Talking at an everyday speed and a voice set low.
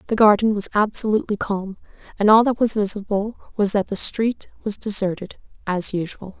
No: average, 170 wpm; high, 205 Hz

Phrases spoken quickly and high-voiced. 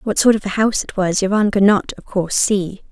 Yes: fast, 270 wpm; high, 200 Hz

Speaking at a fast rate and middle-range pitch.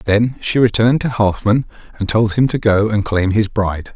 No: fast, 215 wpm; low, 110 Hz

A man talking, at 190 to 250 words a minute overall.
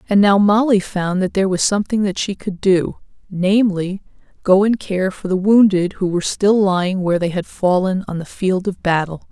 No: female; average, 200 wpm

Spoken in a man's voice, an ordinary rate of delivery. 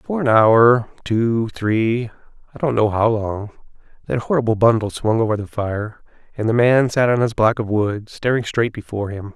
Yes: male; average, 180 wpm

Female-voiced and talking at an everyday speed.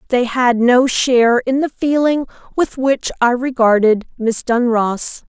Yes: female; average, 145 wpm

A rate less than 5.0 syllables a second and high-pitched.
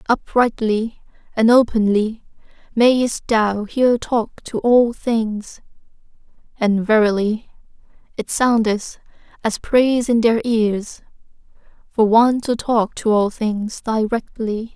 Yes: 3.6 syllables/s; high, 225 Hz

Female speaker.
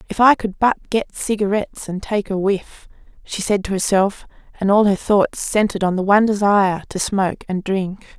Yes: female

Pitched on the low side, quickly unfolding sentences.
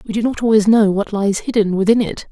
No: high, 210 Hz; fast, 260 wpm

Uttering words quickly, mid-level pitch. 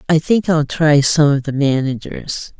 No: average, 185 wpm; medium, 150 Hz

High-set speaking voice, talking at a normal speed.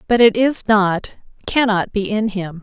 Yes: high, 210 Hz; average, 185 wpm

